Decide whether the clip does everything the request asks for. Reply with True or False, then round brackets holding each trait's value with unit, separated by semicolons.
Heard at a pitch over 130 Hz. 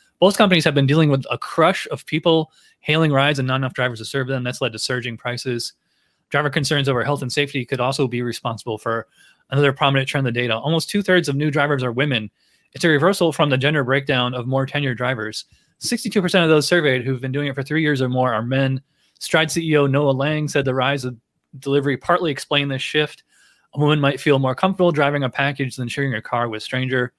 True (140 Hz)